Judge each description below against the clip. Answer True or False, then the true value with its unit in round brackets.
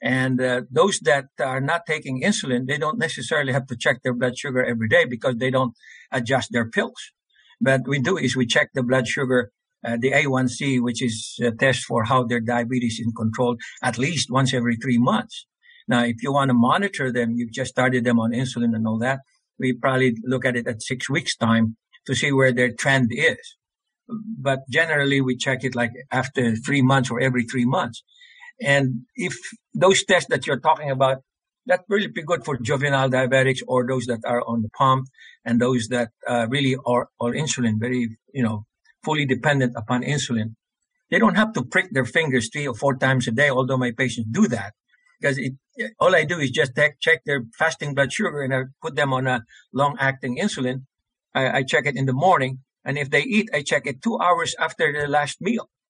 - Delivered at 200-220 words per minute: True (205 wpm)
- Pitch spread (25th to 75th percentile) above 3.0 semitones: False (2.6 semitones)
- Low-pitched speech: True (130 Hz)